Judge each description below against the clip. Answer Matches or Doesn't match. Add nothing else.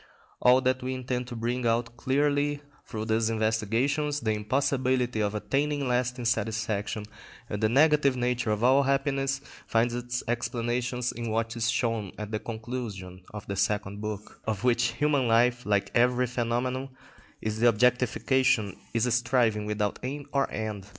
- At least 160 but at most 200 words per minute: Matches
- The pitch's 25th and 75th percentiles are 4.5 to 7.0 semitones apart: Doesn't match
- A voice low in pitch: Matches